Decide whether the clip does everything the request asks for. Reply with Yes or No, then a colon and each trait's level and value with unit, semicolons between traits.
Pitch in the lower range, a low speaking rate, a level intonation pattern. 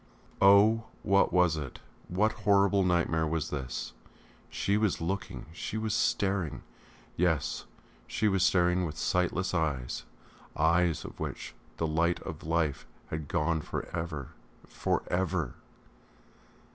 No: very low, 85 Hz; slow, 130 wpm; average, 3.5 semitones